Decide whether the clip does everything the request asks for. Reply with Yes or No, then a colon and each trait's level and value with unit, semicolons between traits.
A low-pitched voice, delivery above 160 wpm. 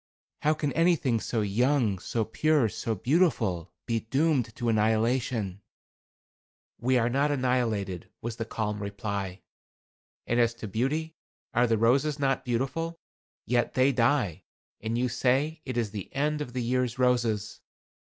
No: low, 120 Hz; average, 145 wpm